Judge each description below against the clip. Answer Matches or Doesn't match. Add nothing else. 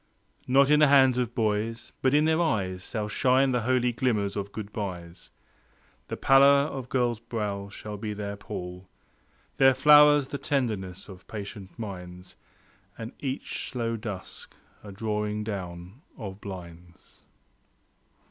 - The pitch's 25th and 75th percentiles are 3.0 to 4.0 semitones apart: Doesn't match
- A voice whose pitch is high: Doesn't match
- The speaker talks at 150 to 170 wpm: Doesn't match